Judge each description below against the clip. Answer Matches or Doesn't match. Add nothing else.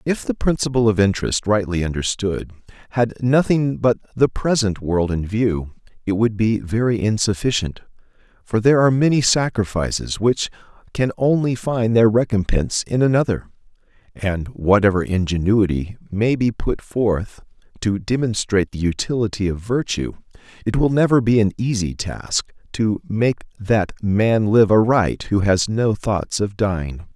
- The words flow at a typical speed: Matches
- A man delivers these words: Matches